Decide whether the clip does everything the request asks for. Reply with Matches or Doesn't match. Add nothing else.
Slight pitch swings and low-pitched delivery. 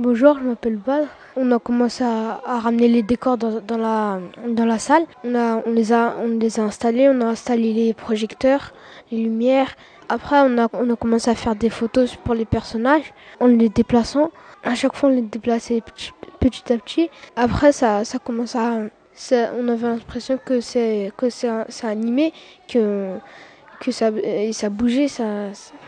Doesn't match